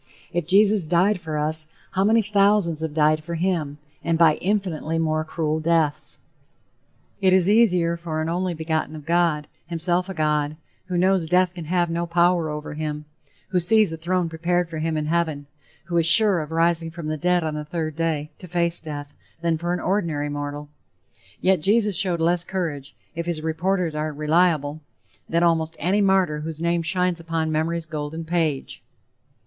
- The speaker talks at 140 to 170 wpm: No, average, 180 wpm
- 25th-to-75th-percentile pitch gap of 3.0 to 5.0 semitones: No, narrow, 2.4 semitones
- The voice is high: No, medium, 165 Hz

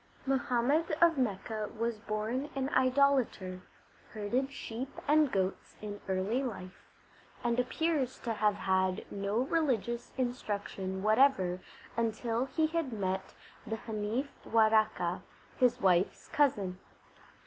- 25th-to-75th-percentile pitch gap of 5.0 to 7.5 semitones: No, average, 4.6 semitones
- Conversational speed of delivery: No, slow, 115 wpm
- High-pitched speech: Yes, high, 225 Hz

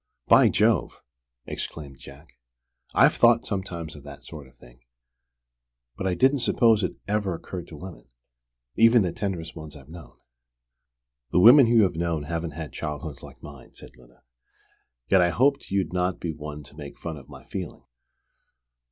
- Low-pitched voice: Yes, very low, 85 Hz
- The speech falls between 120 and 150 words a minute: No, average, 165 wpm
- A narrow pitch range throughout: No, average, 4.5 semitones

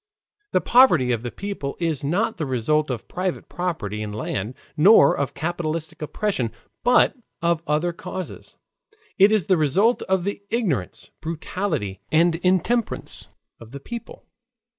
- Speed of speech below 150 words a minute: Yes, average, 140 wpm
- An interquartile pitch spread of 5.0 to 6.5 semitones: Yes, wide, 5.6 semitones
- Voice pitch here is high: No, medium, 165 Hz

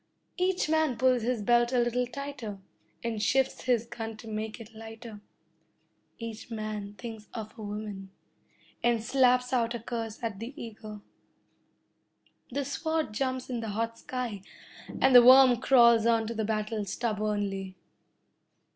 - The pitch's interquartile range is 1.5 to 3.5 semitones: Yes, narrow, 2.6 semitones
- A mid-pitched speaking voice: No, high, 230 Hz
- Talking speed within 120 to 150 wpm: Yes, average, 145 wpm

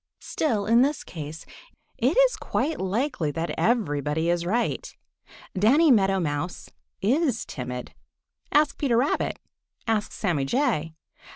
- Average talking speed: No, slow, 120 wpm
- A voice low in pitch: No, high, 205 Hz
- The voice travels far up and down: Yes, wide, 8.2 semitones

